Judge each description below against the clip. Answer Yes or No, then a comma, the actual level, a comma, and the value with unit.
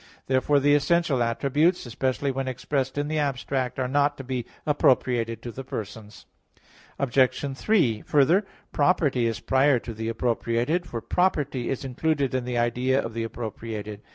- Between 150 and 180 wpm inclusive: Yes, average, 155 wpm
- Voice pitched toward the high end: No, low, 130 Hz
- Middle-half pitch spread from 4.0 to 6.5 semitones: No, average, 3.4 semitones